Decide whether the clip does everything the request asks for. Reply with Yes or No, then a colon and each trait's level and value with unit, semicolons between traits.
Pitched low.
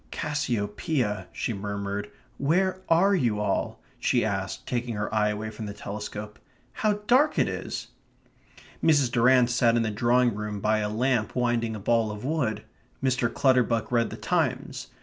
Yes: low, 115 Hz